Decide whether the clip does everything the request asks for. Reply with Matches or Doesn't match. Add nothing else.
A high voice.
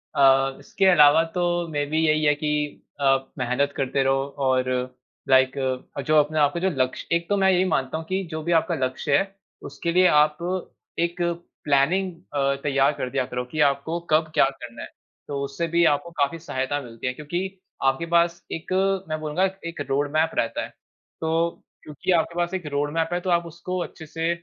Doesn't match